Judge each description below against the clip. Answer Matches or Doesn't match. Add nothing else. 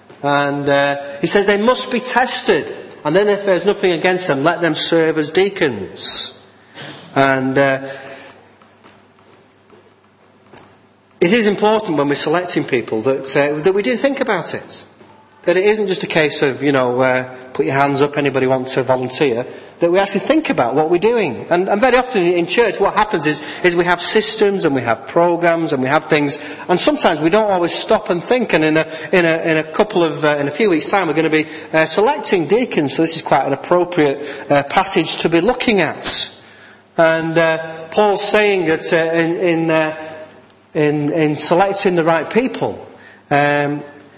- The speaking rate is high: Doesn't match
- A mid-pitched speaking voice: Matches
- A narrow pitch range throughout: Doesn't match